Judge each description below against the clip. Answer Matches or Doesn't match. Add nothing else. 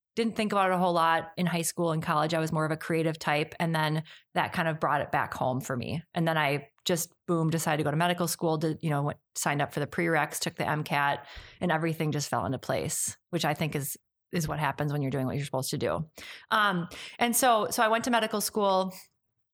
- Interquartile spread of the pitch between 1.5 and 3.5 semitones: Matches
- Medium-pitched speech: Matches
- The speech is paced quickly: Matches